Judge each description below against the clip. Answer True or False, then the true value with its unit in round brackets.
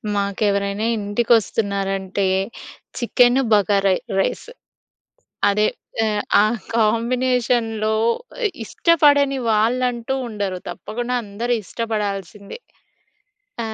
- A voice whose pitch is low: False (215 Hz)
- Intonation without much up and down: False (3.2 semitones)